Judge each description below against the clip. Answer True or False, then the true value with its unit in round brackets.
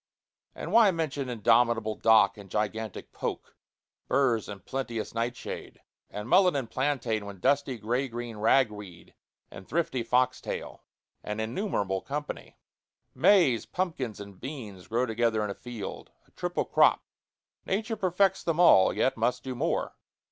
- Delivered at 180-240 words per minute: False (140 wpm)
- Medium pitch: False (120 Hz)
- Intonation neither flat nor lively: True (4.6 semitones)